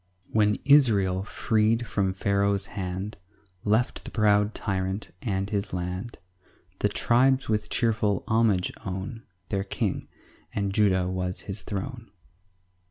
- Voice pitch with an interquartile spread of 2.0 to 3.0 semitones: Yes, average, 2.7 semitones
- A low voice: Yes, low, 100 Hz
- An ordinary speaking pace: No, slow, 125 wpm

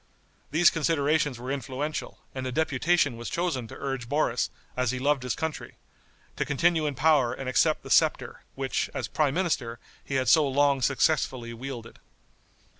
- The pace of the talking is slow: No, average, 165 wpm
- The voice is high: No, low, 135 Hz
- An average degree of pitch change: Yes, average, 3.2 semitones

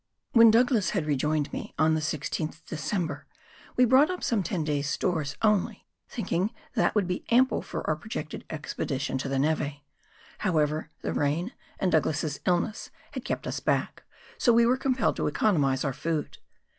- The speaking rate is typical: Yes, average, 170 wpm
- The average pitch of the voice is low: No, medium, 160 Hz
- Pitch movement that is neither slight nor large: No, wide, 6.4 semitones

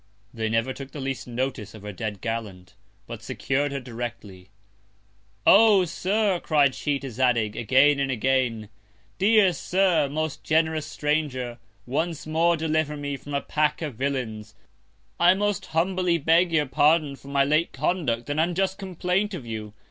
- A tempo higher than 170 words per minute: No, average, 155 wpm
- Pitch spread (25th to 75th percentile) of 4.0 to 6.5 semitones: Yes, wide, 5.4 semitones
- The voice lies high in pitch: No, medium, 145 Hz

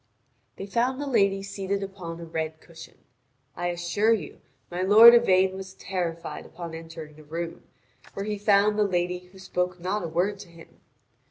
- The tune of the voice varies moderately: Yes, average, 3.0 semitones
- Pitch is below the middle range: No, medium, 185 Hz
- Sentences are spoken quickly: No, average, 175 wpm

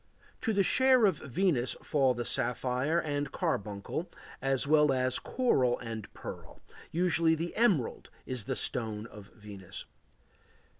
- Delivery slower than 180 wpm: Yes, slow, 135 wpm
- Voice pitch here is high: No, low, 135 Hz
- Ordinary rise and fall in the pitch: No, wide, 6.1 semitones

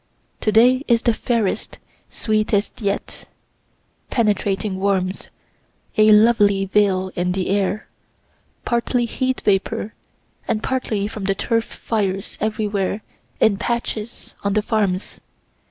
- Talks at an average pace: No, slow, 115 wpm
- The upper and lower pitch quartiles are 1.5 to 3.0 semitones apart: Yes, narrow, 2.4 semitones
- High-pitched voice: Yes, high, 210 Hz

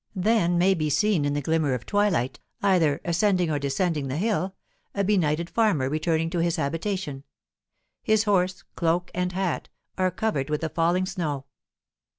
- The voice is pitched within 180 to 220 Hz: No, medium, 170 Hz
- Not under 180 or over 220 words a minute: No, average, 165 wpm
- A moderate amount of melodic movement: Yes, average, 4.0 semitones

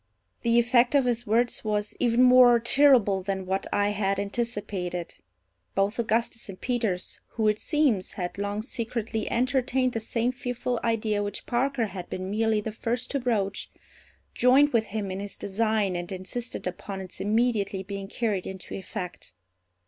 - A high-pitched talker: Yes, high, 220 Hz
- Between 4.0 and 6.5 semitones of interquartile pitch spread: No, average, 3.6 semitones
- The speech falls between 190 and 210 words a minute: No, average, 160 wpm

